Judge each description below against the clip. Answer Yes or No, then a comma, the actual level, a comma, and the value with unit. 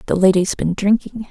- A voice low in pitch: No, high, 200 Hz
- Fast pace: No, average, 185 wpm